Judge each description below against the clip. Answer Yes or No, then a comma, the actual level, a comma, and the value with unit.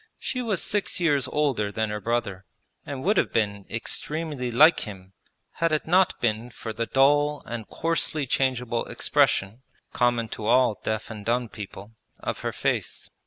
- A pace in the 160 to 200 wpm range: Yes, average, 165 wpm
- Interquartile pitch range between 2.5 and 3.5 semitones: No, average, 5.2 semitones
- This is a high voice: No, low, 120 Hz